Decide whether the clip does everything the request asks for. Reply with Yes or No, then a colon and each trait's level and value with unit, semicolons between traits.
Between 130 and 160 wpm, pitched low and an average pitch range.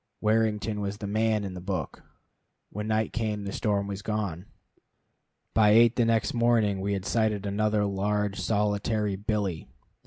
No: average, 155 wpm; low, 105 Hz; narrow, 1.5 semitones